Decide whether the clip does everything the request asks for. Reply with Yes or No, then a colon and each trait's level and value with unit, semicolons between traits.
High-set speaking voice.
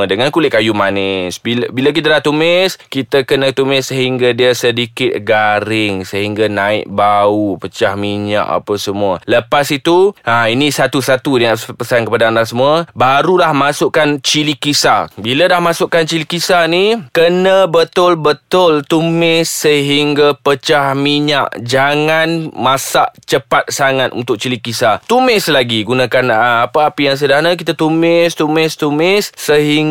No: medium, 140 Hz